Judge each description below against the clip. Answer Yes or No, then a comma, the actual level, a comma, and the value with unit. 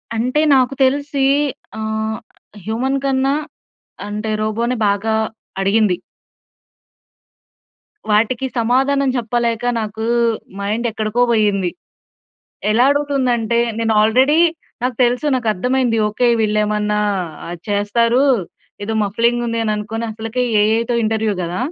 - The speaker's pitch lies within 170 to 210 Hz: No, high, 225 Hz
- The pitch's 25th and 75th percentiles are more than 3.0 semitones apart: No, average, 2.7 semitones